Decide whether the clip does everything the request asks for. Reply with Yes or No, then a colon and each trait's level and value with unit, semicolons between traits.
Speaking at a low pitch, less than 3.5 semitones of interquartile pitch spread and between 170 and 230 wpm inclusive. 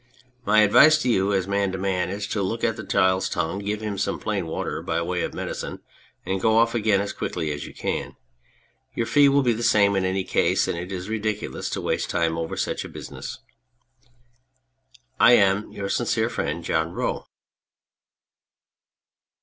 Yes: low, 100 Hz; average, 2.9 semitones; average, 180 wpm